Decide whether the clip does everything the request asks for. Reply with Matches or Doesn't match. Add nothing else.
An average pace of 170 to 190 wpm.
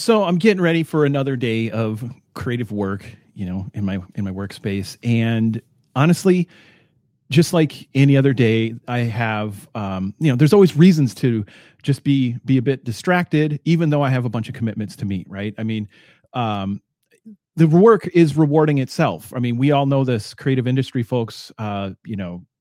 Matches